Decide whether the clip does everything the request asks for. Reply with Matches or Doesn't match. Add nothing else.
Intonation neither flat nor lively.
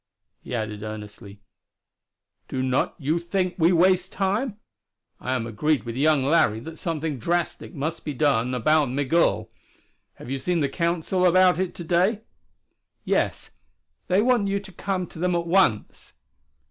Doesn't match